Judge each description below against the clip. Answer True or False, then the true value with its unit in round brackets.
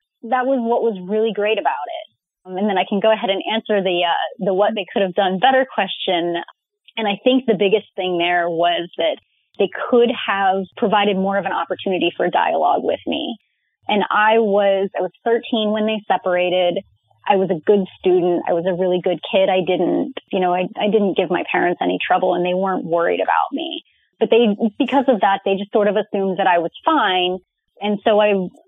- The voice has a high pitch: True (200 Hz)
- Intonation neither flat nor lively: True (3.3 semitones)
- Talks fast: True (215 wpm)